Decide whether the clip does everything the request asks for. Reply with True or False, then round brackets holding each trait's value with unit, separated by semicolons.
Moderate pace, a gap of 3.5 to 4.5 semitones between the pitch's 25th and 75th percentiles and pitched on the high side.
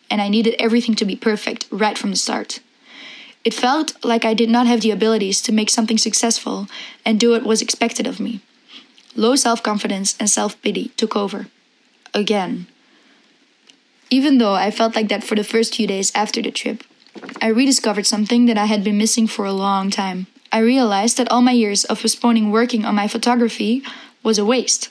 False (195 wpm; 2.7 semitones; 230 Hz)